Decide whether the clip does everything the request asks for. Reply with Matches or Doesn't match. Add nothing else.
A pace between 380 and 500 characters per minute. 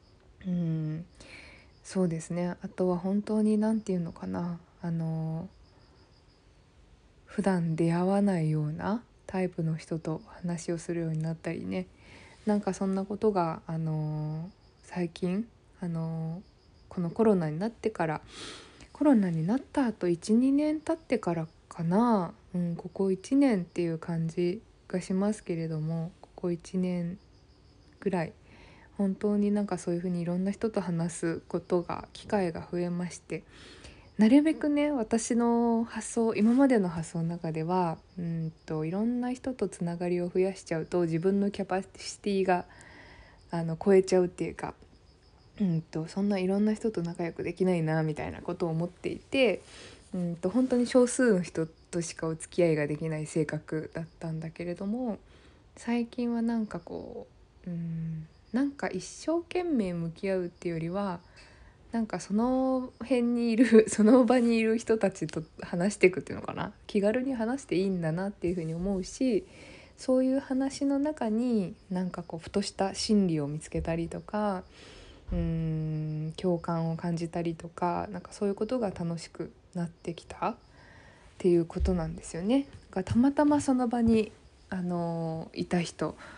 Doesn't match